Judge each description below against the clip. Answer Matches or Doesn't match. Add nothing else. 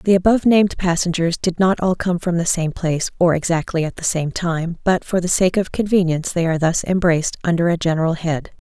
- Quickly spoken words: Matches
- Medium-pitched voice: Matches